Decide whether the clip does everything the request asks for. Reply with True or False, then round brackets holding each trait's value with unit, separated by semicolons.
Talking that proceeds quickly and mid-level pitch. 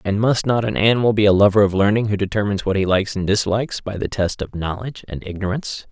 False (245 wpm; 105 Hz)